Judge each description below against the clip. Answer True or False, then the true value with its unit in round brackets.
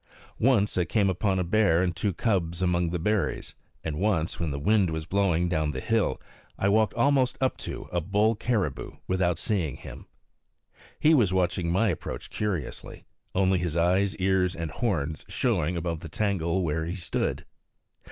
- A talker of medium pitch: False (90 Hz)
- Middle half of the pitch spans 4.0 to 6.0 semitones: False (3.6 semitones)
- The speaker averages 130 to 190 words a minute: True (170 wpm)